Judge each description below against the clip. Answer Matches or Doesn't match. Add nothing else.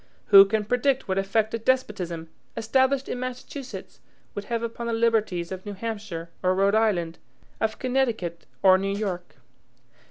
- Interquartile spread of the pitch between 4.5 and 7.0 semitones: Doesn't match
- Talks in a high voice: Matches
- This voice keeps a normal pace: Matches